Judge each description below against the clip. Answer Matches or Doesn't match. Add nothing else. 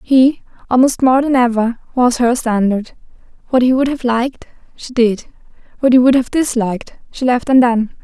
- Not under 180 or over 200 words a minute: Doesn't match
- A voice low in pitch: Doesn't match